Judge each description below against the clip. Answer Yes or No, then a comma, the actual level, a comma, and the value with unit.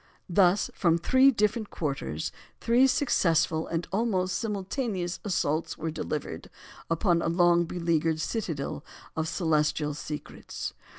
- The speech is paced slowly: Yes, slow, 115 wpm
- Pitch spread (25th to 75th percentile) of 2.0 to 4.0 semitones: No, average, 4.4 semitones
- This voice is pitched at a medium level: Yes, medium, 170 Hz